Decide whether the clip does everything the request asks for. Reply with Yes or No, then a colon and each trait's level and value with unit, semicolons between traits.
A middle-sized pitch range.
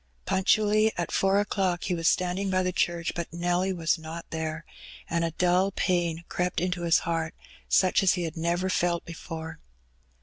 No: narrow, 1.9 semitones